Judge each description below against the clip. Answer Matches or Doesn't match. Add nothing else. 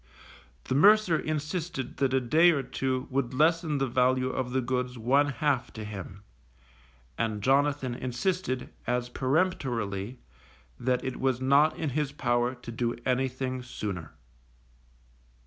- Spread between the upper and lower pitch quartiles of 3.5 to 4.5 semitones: Doesn't match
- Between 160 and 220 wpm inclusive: Doesn't match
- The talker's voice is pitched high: Doesn't match